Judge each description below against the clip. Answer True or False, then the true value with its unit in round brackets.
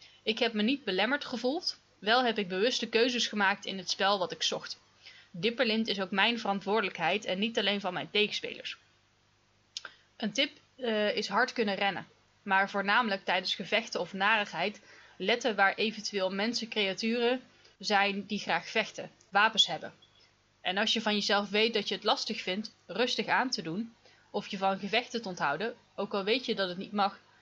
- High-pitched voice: True (210 Hz)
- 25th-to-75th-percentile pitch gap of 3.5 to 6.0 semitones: False (2.7 semitones)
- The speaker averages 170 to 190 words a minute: True (175 wpm)